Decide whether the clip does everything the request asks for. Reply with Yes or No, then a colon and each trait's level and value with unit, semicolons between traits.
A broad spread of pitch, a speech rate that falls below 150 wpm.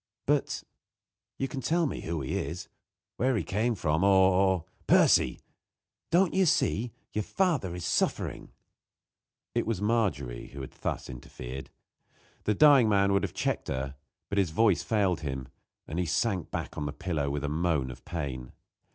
No: wide, 7.3 semitones; average, 170 wpm